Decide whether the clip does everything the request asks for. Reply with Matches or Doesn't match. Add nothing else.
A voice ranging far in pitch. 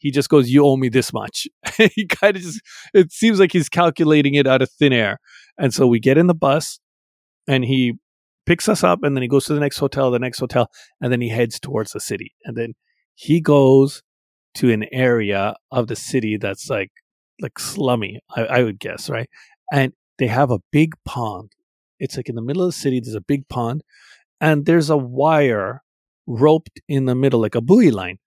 Doesn't match